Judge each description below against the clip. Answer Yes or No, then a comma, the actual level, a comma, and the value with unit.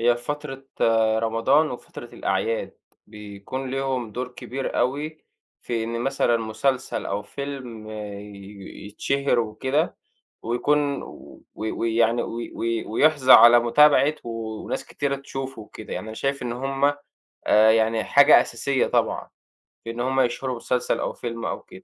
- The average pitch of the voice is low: Yes, low, 120 Hz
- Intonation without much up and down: No, average, 3.3 semitones